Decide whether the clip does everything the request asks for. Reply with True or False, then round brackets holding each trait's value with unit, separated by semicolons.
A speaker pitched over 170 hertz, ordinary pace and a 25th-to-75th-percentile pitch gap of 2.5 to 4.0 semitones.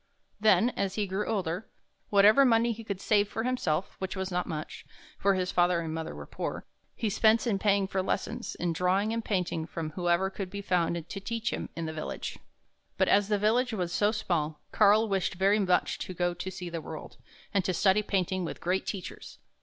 False (190 Hz; 215 wpm; 3.0 semitones)